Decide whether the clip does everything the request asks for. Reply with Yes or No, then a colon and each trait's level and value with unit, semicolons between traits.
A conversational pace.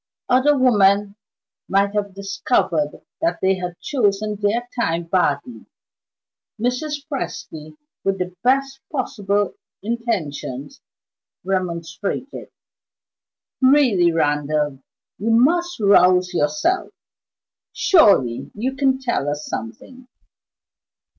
No: slow, 90 wpm